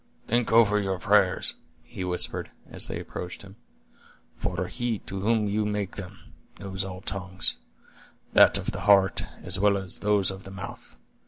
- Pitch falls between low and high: No, very low, 95 Hz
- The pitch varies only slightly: Yes, narrow, 1.8 semitones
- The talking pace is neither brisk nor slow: Yes, average, 165 wpm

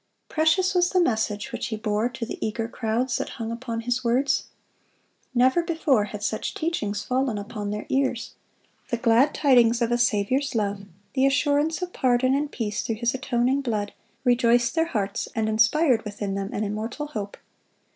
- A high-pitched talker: Yes, high, 240 Hz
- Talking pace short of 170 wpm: No, average, 175 wpm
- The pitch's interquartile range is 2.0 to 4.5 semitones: Yes, average, 3.9 semitones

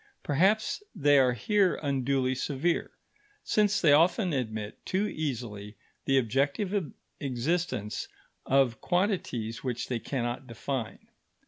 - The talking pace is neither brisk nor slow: No, slow, 110 wpm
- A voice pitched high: No, low, 135 Hz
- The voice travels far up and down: Yes, wide, 6.2 semitones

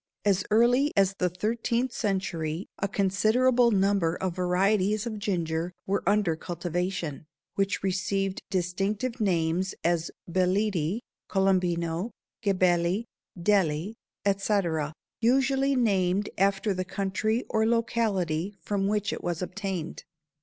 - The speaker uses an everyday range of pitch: Yes, average, 3.0 semitones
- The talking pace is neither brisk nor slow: No, slow, 110 wpm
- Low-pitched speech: No, high, 195 Hz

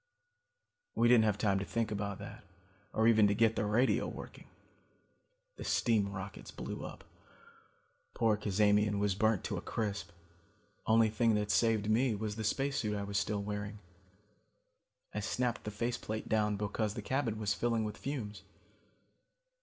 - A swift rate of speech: No, average, 160 wpm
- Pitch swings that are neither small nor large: No, narrow, 1.7 semitones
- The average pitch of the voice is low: Yes, low, 105 Hz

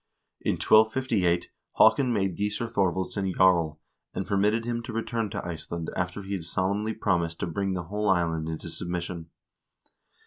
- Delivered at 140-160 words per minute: Yes, average, 150 wpm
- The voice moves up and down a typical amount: Yes, average, 3.6 semitones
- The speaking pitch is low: Yes, very low, 95 Hz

